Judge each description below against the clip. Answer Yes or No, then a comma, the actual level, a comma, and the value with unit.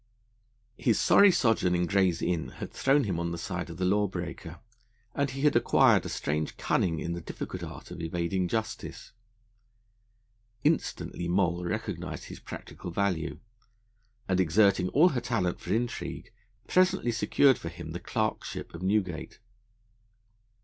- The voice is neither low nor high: No, very low, 95 Hz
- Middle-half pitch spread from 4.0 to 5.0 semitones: Yes, average, 4.5 semitones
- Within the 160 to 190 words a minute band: No, average, 150 wpm